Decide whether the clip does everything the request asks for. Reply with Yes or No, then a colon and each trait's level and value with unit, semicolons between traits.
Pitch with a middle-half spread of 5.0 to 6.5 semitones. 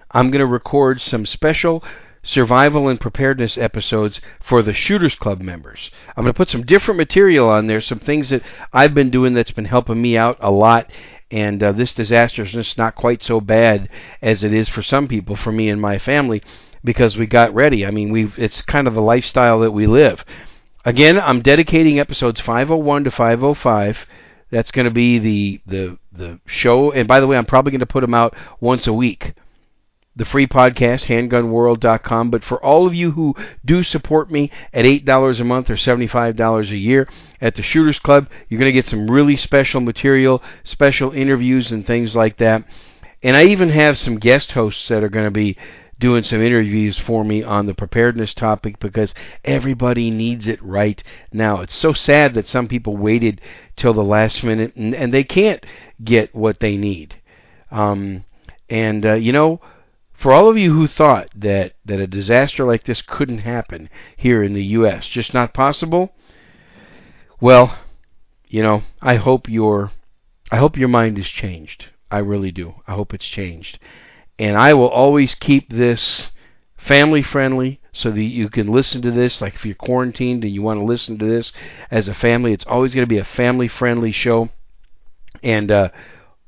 No: average, 3.4 semitones